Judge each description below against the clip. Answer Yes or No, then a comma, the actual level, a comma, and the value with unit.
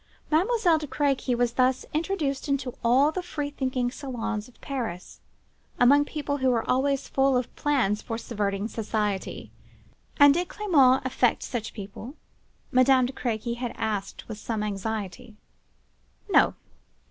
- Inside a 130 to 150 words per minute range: Yes, average, 140 wpm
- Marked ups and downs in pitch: No, average, 4.0 semitones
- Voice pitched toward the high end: Yes, very high, 255 Hz